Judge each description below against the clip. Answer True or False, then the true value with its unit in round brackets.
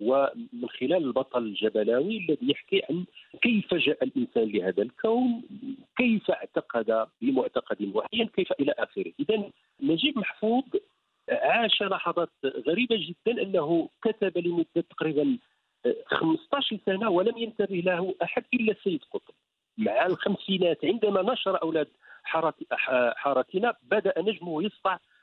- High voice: True (215 Hz)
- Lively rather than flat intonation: True (6.8 semitones)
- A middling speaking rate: False (115 wpm)